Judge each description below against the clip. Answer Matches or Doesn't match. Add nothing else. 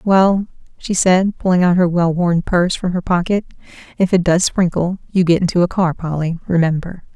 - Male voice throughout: Doesn't match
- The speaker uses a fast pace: Doesn't match